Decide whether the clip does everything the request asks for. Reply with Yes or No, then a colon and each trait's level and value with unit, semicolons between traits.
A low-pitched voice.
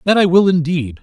No: medium, 170 Hz